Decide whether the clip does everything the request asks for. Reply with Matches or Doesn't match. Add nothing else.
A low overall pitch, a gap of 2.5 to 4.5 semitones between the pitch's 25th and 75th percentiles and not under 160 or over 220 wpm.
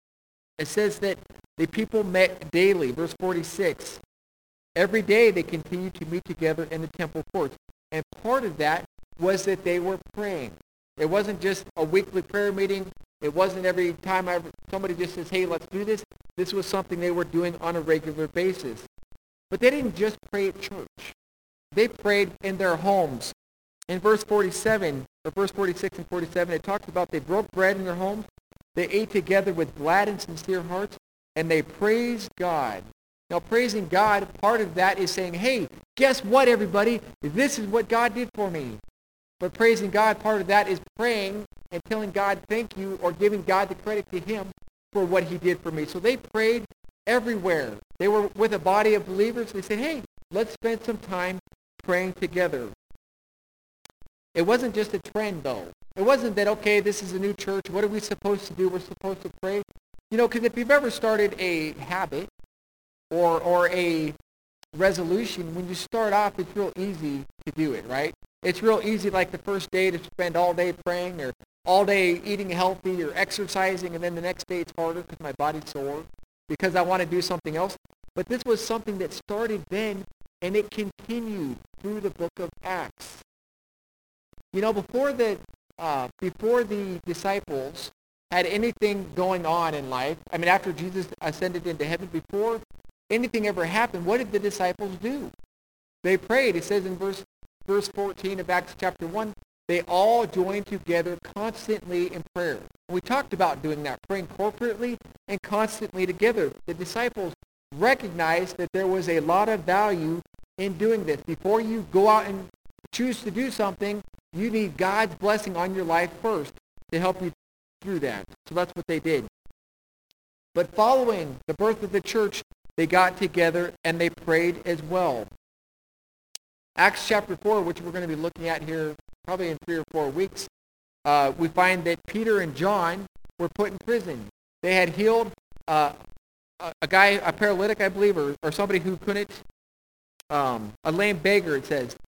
Doesn't match